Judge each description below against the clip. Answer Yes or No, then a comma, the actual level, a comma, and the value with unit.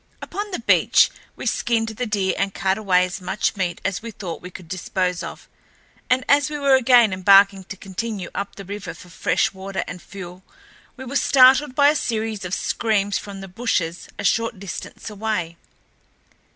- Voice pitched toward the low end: No, high, 200 Hz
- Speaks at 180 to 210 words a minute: Yes, average, 185 wpm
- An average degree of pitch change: Yes, average, 3.8 semitones